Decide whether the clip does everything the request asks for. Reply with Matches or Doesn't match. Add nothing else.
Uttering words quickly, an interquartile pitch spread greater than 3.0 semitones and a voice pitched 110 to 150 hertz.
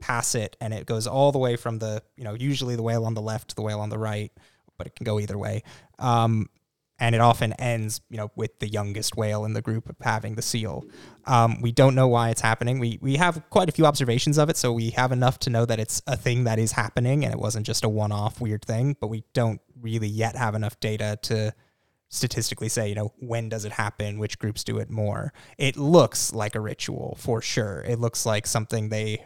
Doesn't match